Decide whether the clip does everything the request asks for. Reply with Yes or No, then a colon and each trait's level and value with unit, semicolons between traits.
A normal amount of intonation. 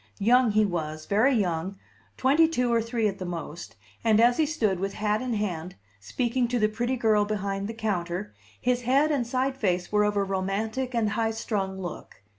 Yes: average, 4.0 semitones